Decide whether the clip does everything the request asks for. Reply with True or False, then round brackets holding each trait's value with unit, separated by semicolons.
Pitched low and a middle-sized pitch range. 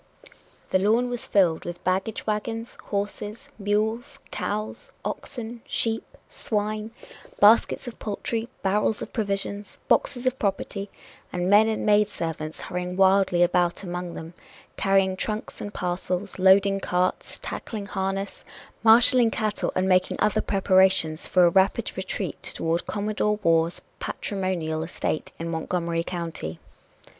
False (195 Hz; 3.1 semitones)